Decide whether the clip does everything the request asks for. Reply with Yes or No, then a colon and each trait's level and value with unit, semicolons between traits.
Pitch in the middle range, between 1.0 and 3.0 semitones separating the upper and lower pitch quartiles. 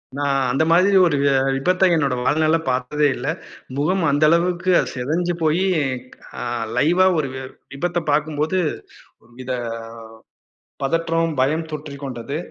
No: medium, 155 Hz; average, 3.5 semitones